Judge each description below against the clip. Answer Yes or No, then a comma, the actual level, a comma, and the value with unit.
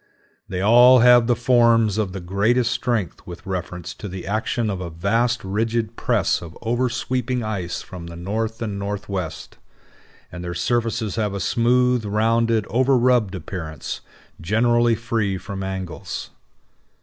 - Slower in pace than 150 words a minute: Yes, average, 140 wpm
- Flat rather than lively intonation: No, average, 3.9 semitones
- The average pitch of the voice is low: Yes, low, 110 Hz